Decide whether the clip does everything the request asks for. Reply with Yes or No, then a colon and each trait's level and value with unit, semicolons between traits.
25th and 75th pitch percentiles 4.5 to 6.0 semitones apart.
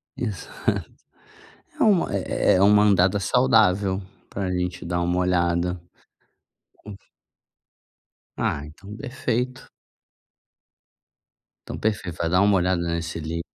No: average, 3.1 semitones